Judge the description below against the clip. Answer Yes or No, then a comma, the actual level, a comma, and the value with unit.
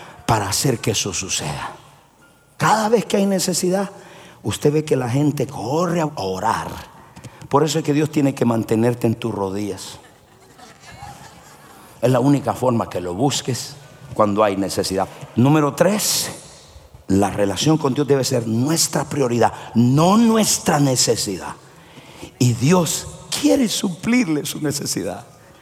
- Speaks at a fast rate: No, average, 135 wpm